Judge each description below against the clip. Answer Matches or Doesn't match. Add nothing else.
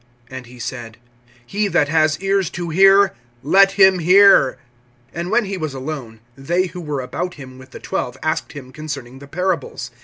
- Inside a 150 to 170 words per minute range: Doesn't match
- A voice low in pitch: Doesn't match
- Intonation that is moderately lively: Doesn't match